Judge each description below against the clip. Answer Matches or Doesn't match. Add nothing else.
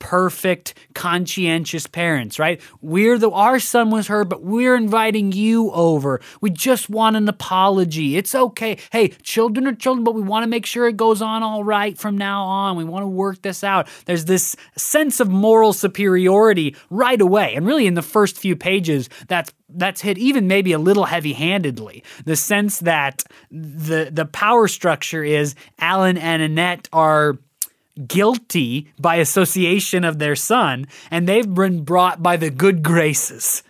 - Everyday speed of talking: Matches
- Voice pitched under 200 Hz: Matches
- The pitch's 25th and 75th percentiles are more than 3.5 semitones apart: Matches